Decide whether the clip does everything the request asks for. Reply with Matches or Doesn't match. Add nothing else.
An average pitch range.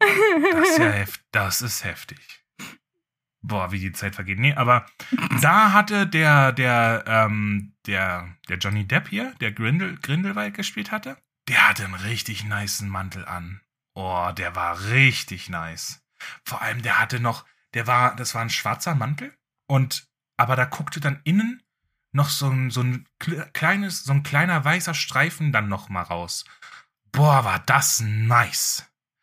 Doesn't match